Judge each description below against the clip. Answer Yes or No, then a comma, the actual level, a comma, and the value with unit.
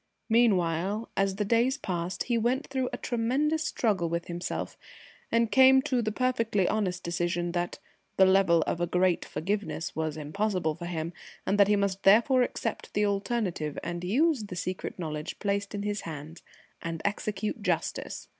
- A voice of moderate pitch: No, high, 195 Hz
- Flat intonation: No, average, 4.8 semitones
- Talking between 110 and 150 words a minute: No, average, 165 wpm